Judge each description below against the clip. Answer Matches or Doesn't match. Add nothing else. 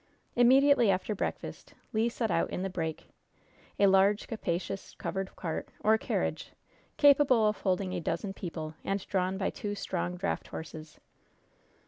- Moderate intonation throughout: Matches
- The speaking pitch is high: Matches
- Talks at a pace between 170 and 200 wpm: Doesn't match